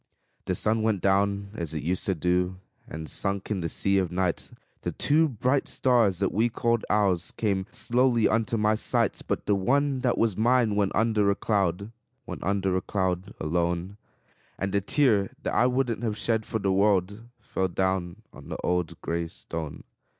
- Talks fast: No, average, 185 wpm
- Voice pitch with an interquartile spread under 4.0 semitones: Yes, average, 3.6 semitones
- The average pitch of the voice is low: Yes, low, 100 Hz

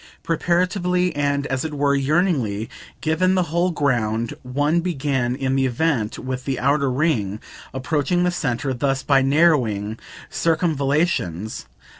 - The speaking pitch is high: No, medium, 140 Hz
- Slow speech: Yes, slow, 130 wpm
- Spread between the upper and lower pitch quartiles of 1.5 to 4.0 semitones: No, average, 4.5 semitones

